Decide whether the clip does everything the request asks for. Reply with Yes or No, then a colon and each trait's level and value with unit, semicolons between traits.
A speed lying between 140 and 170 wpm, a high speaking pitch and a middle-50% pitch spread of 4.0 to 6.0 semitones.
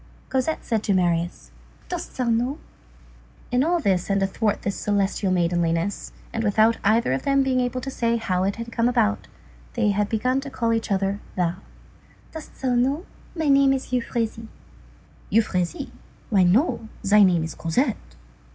Yes: average, 165 wpm; high, 225 Hz; average, 4.6 semitones